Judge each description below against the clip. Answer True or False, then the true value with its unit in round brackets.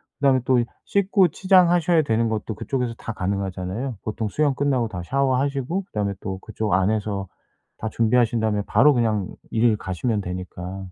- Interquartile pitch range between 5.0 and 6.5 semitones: True (5.3 semitones)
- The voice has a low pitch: True (115 Hz)